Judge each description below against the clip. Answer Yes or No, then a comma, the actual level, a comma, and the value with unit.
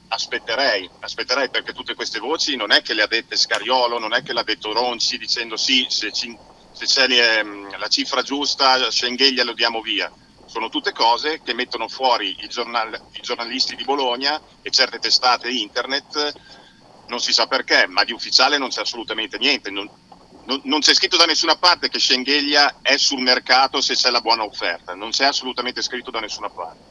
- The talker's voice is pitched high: No, low, 130 Hz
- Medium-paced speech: No, fast, 185 wpm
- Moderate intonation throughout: Yes, average, 3.3 semitones